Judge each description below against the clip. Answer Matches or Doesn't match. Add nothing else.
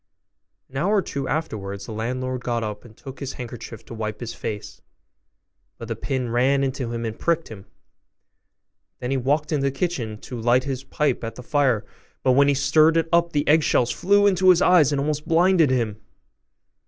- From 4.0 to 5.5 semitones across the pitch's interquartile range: Matches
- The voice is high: Doesn't match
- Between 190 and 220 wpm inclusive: Matches